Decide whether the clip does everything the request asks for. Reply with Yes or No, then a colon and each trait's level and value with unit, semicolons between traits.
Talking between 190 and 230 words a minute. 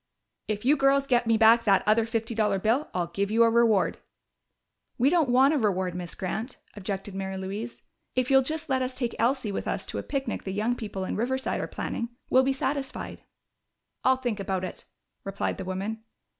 Yes: average, 200 wpm